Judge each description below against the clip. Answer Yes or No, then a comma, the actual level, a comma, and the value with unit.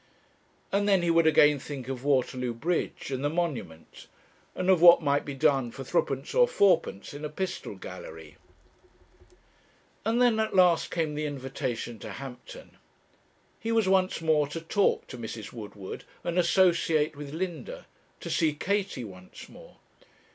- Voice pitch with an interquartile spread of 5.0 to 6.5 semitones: Yes, wide, 5.6 semitones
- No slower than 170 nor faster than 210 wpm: No, average, 155 wpm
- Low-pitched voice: No, medium, 155 Hz